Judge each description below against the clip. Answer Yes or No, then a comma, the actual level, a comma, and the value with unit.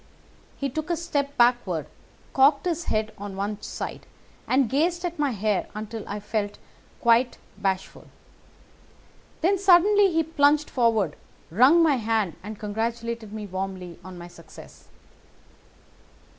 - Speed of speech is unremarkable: No, slow, 130 wpm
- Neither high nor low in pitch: No, high, 230 Hz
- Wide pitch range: Yes, wide, 6.6 semitones